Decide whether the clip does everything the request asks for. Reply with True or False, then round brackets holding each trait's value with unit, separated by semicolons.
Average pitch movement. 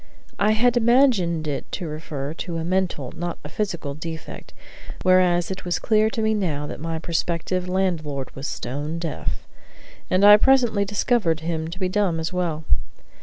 True (4.1 semitones)